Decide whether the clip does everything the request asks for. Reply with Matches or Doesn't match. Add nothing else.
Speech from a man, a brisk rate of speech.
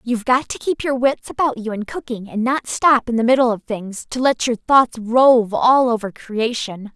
Doesn't match